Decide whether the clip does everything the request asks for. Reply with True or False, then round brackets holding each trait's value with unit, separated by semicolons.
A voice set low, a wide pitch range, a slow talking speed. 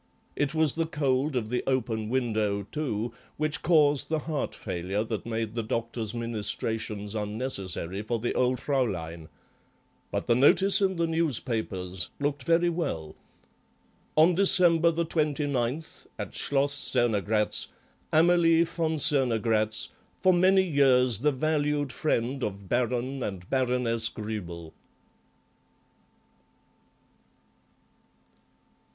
True (125 Hz; 5.8 semitones; 110 wpm)